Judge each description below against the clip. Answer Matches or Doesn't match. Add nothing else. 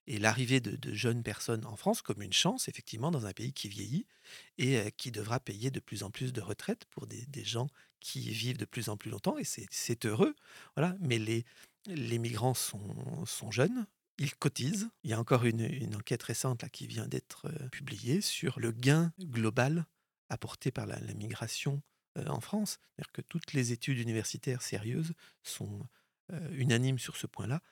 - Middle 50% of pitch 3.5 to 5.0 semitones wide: Matches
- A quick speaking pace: Doesn't match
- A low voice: Matches